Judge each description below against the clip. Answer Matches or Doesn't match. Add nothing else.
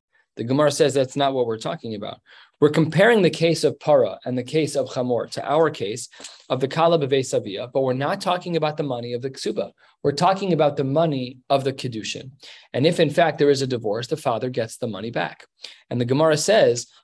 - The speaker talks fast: Matches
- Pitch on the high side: Doesn't match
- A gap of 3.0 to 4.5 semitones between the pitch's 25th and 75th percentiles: Matches